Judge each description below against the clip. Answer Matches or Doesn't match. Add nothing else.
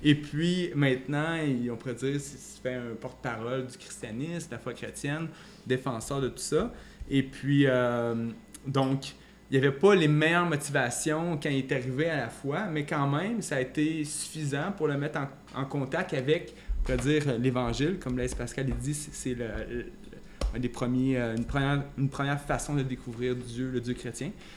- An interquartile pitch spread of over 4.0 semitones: Doesn't match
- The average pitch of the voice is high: Doesn't match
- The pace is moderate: Matches